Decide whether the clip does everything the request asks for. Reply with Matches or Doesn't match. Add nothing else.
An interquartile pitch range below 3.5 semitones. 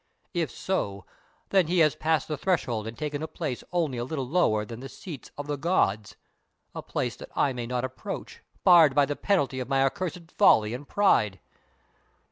Doesn't match